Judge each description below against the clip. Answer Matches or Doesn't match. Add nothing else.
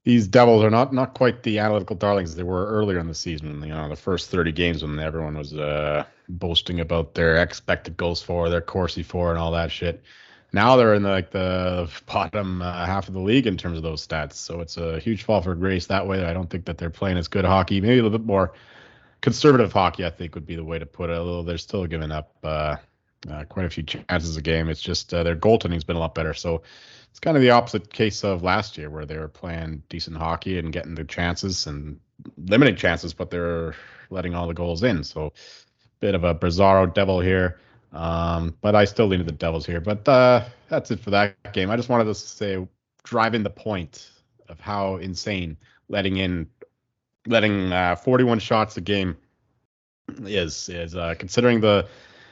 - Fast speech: Matches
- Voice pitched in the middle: Doesn't match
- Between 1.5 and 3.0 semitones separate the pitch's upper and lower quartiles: Doesn't match